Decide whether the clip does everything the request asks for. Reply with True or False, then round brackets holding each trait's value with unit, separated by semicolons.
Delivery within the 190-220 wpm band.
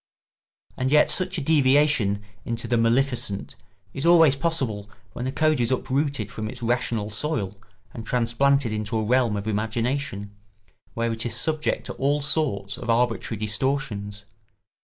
False (150 wpm)